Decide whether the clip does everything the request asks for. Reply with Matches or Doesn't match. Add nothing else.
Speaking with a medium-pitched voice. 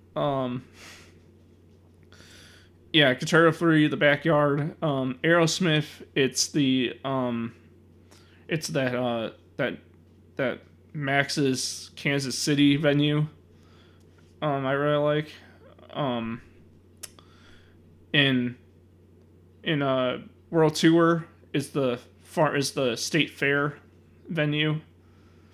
Doesn't match